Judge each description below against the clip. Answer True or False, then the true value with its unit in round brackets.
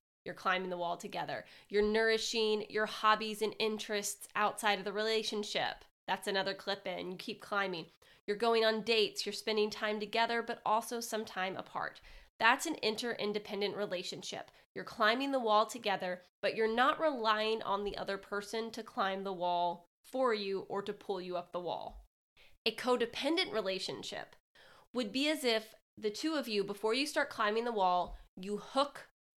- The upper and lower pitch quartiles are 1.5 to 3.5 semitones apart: True (2.6 semitones)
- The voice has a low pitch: False (215 Hz)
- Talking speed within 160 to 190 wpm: True (170 wpm)